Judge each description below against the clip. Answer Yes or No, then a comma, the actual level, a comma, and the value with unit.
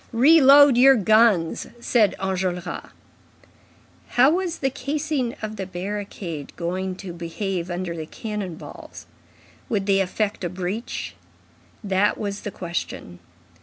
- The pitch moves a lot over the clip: No, average, 4.8 semitones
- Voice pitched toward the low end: No, high, 200 Hz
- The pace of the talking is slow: Yes, slow, 125 wpm